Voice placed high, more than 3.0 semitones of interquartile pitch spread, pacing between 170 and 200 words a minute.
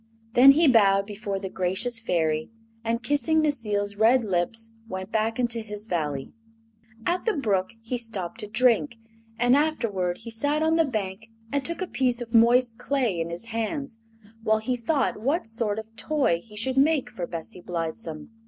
Yes: high, 225 Hz; average, 4.5 semitones; average, 175 wpm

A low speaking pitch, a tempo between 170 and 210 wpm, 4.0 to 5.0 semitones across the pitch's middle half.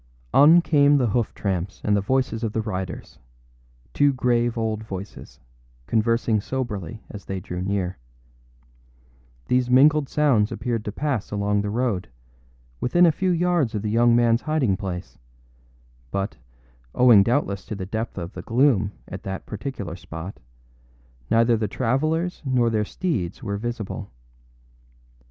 No: low, 115 Hz; average, 145 wpm; average, 4.5 semitones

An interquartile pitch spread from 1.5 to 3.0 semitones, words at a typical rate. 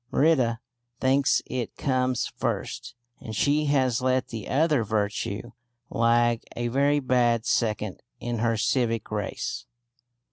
No: narrow, 2.5 semitones; slow, 120 wpm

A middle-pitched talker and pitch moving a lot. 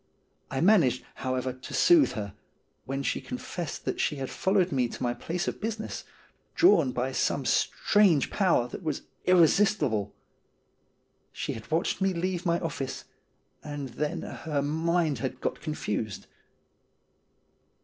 Yes: medium, 155 Hz; wide, 5.9 semitones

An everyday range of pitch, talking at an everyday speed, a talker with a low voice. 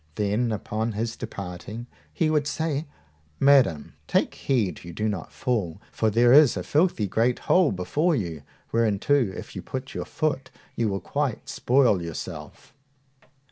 No: wide, 5.8 semitones; average, 150 wpm; low, 115 Hz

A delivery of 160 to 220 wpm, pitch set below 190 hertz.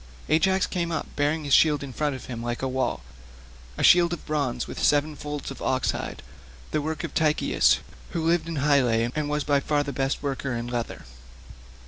Yes: average, 190 wpm; medium, 140 Hz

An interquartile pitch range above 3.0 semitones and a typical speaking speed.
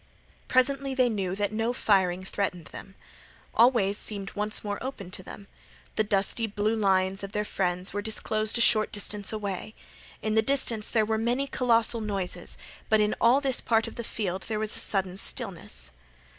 No: average, 2.7 semitones; average, 185 wpm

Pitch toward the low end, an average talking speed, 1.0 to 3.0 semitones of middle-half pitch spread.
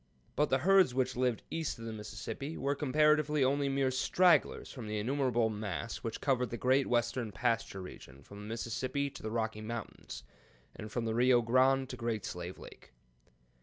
No: low, 125 Hz; average, 180 wpm; average, 3.6 semitones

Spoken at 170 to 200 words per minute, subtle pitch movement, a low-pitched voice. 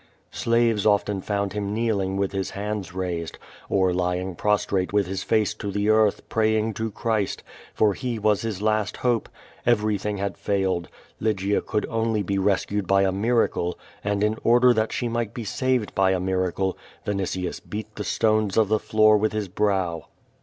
Yes: average, 175 wpm; narrow, 2.1 semitones; low, 105 Hz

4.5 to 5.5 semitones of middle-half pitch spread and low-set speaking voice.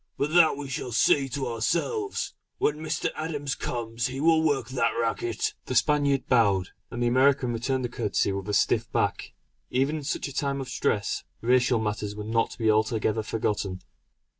No: average, 4.0 semitones; low, 125 Hz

